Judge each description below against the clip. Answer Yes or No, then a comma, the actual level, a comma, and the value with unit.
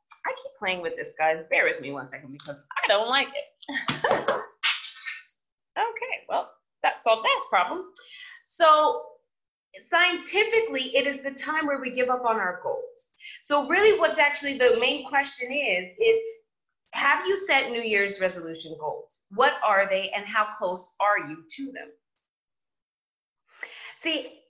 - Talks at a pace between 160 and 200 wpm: No, average, 150 wpm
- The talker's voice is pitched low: No, very high, 280 Hz